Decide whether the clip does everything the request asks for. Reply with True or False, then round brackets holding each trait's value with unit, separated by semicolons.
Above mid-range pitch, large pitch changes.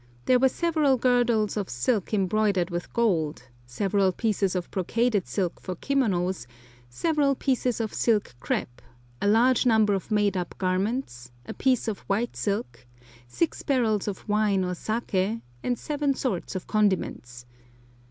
False (210 Hz; 4.7 semitones)